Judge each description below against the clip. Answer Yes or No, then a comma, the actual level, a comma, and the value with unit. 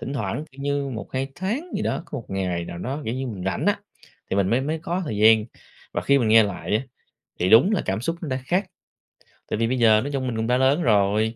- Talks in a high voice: No, low, 120 Hz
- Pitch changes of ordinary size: Yes, average, 4.8 semitones